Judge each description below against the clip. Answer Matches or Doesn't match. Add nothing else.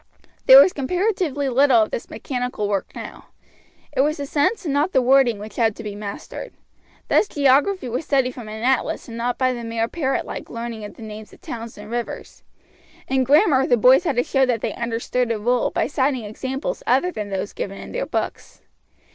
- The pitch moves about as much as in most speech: Matches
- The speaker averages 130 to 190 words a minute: Doesn't match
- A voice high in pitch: Matches